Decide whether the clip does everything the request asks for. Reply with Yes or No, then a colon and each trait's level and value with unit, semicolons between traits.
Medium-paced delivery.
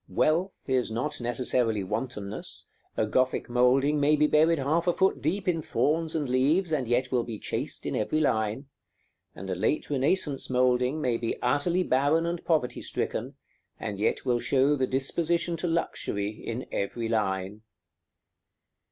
Yes: average, 160 wpm